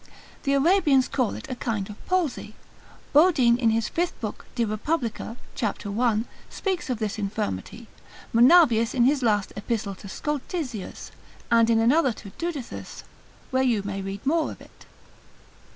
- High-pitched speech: Yes, high, 235 Hz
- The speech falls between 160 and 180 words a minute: No, average, 150 wpm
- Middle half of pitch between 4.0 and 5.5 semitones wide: Yes, average, 4.8 semitones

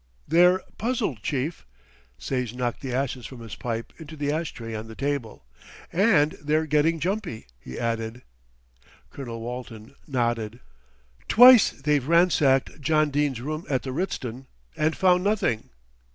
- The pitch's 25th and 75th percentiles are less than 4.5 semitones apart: No, average, 5.1 semitones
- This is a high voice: No, medium, 140 Hz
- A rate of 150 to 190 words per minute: No, average, 140 wpm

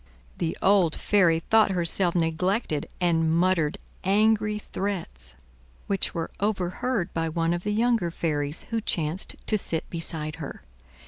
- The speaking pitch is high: No, medium, 175 Hz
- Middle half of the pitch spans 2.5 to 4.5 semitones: Yes, average, 3.8 semitones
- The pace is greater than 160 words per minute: No, slow, 135 wpm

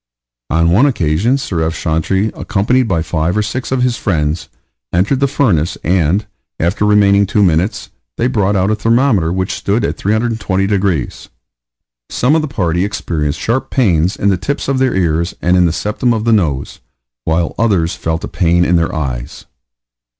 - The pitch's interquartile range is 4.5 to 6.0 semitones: Yes, average, 5.0 semitones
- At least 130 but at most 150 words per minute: No, average, 180 wpm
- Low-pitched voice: Yes, very low, 95 Hz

